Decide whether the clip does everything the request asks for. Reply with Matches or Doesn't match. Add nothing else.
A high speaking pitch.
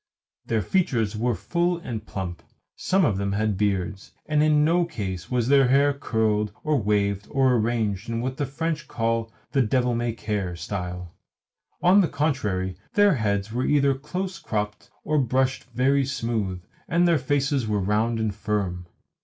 Doesn't match